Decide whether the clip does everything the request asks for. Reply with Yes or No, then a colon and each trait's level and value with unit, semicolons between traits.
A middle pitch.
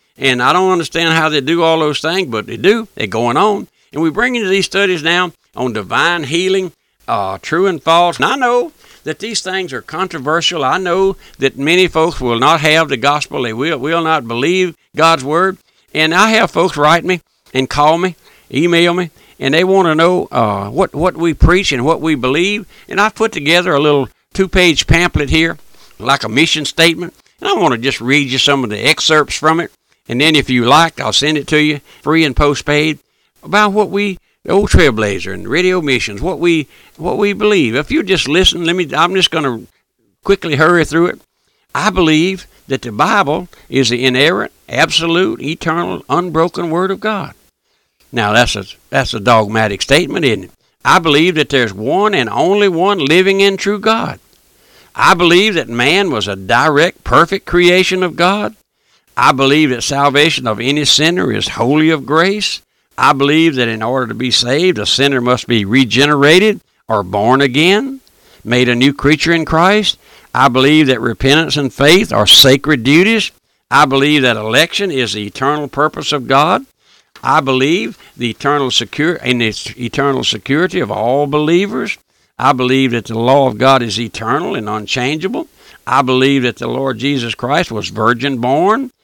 Yes: medium, 155 Hz